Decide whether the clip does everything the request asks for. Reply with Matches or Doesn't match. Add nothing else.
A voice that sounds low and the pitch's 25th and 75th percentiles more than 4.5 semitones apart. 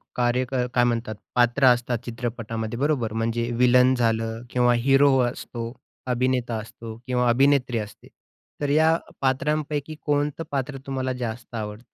Doesn't match